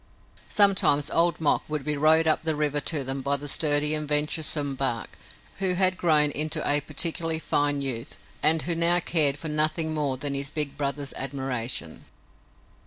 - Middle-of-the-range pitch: Yes, medium, 150 Hz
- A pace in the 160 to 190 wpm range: Yes, average, 175 wpm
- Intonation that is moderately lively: No, narrow, 2.2 semitones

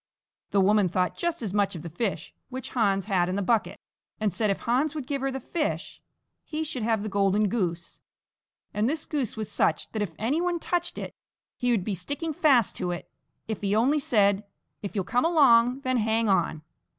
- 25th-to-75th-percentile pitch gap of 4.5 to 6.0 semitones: Yes, wide, 5.4 semitones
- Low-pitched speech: No, high, 220 Hz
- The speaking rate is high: Yes, fast, 210 wpm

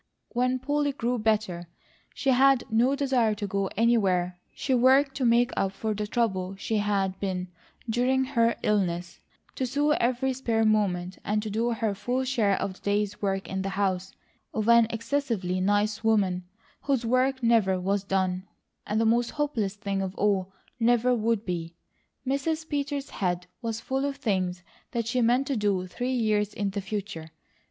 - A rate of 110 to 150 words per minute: No, average, 170 wpm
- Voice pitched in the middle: No, high, 220 Hz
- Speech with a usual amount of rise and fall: Yes, average, 4.3 semitones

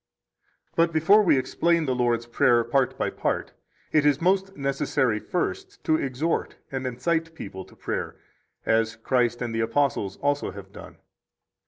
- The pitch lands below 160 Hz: Yes, low, 135 Hz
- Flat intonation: No, wide, 5.5 semitones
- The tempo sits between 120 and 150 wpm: No, average, 160 wpm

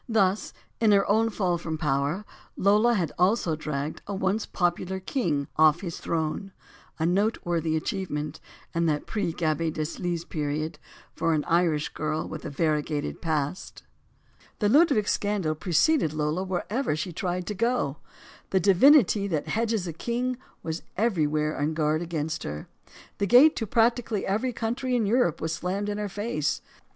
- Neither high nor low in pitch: Yes, medium, 175 Hz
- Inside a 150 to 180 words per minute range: Yes, average, 160 wpm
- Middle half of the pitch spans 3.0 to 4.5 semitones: No, average, 5.2 semitones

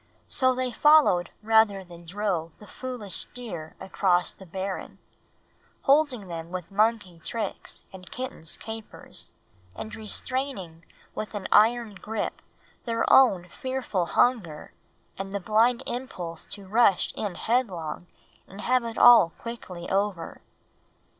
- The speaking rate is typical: No, slow, 125 wpm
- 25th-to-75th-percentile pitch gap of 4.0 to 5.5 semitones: Yes, average, 5.0 semitones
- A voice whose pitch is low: No, high, 205 Hz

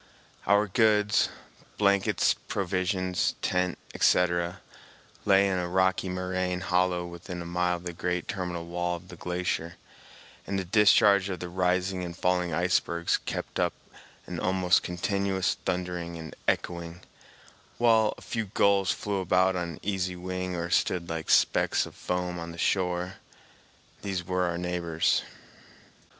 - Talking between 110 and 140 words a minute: Yes, slow, 135 wpm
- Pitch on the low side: Yes, very low, 90 Hz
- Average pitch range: No, narrow, 1.4 semitones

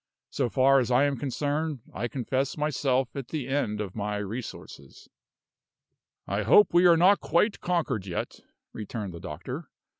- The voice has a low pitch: Yes, low, 130 Hz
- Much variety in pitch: Yes, wide, 5.9 semitones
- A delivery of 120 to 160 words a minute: Yes, average, 155 wpm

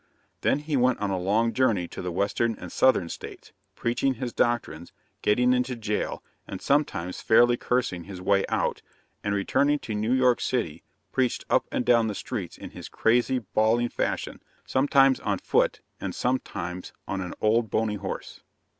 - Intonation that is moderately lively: Yes, average, 4.1 semitones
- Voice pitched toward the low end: Yes, low, 115 Hz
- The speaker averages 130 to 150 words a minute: No, average, 170 wpm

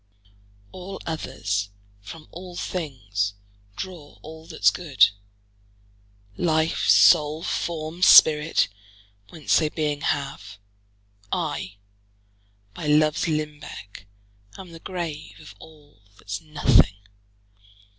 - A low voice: No, medium, 155 Hz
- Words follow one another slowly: Yes, slow, 95 wpm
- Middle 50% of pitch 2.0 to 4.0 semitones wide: Yes, average, 2.9 semitones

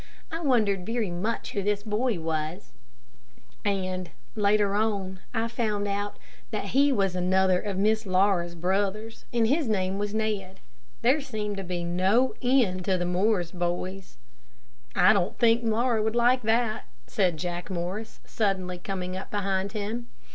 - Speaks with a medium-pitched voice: No, high, 200 Hz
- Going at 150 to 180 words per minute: Yes, average, 155 wpm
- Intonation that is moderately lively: Yes, average, 3.2 semitones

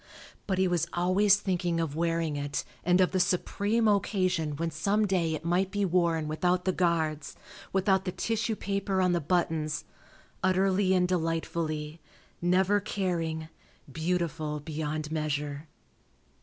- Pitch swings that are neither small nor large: Yes, average, 3.0 semitones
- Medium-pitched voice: Yes, medium, 175 Hz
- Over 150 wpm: No, average, 140 wpm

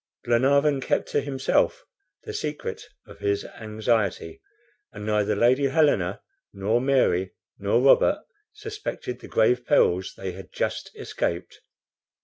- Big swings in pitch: Yes, wide, 5.8 semitones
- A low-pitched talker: Yes, low, 125 Hz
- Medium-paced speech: No, slow, 125 wpm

